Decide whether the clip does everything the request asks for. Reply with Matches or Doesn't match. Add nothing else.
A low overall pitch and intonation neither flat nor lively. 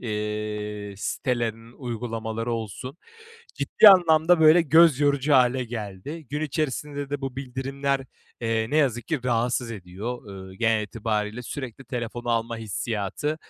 Matches